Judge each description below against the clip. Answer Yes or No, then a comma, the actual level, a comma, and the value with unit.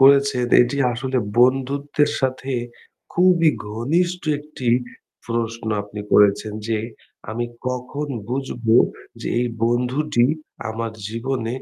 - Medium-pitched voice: No, low, 125 Hz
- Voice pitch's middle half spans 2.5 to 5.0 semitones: Yes, average, 3.3 semitones